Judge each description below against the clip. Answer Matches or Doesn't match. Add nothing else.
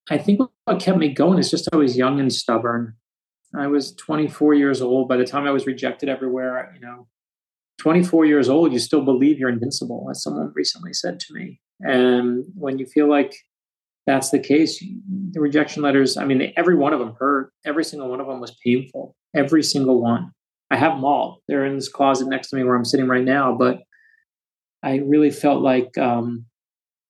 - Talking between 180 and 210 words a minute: Matches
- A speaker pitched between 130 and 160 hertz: Matches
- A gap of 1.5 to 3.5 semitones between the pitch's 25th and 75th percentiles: Matches